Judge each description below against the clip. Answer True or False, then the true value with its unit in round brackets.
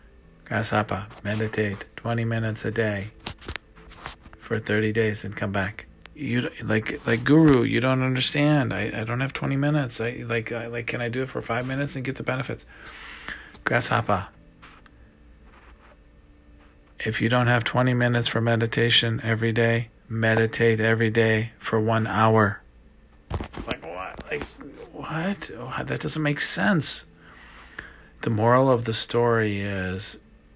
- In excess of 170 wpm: False (145 wpm)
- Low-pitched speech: True (115 Hz)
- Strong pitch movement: False (2.8 semitones)